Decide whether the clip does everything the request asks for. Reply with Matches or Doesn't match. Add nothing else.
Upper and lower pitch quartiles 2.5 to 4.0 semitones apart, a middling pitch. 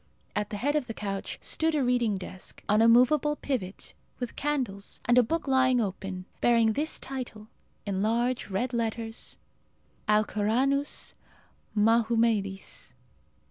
Doesn't match